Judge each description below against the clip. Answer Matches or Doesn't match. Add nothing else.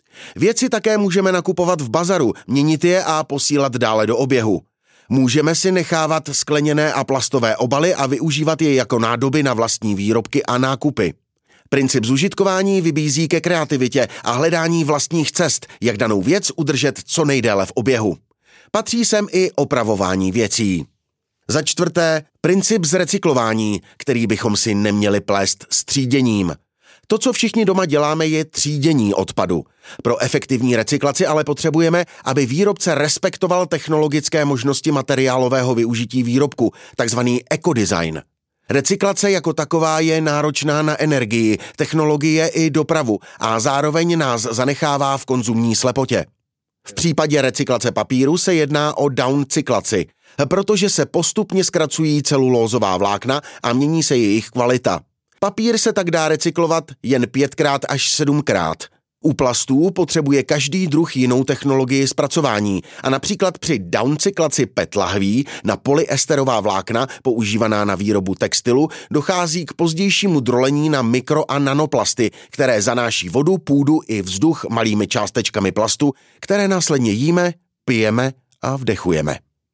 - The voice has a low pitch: Doesn't match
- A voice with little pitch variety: Doesn't match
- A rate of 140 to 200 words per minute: Doesn't match